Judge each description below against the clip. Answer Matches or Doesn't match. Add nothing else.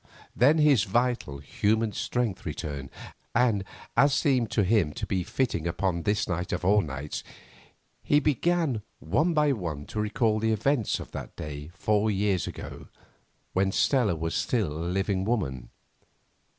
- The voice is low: Matches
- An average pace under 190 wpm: Matches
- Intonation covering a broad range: Matches